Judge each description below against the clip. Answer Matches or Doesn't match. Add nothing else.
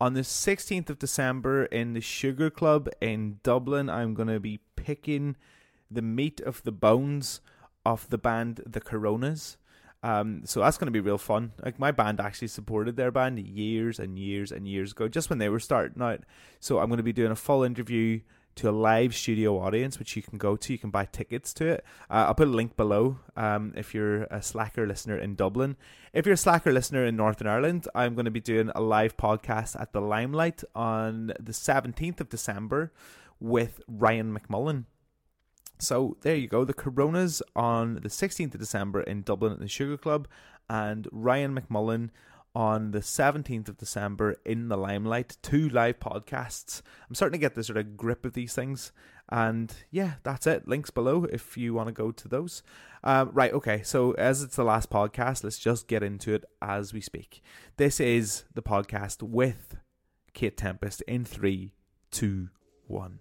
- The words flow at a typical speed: Matches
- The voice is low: Matches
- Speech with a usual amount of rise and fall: Matches